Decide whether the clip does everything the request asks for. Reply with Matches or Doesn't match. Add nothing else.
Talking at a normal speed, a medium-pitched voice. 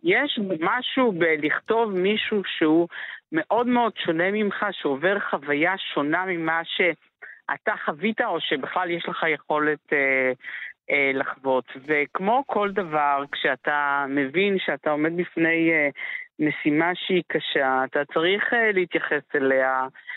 Matches